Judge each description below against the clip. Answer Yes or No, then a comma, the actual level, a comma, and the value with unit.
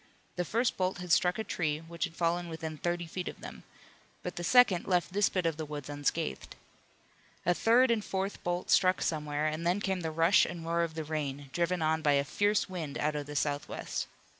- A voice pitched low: No, medium, 170 Hz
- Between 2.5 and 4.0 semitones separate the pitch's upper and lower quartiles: Yes, average, 2.9 semitones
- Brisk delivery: Yes, fast, 220 wpm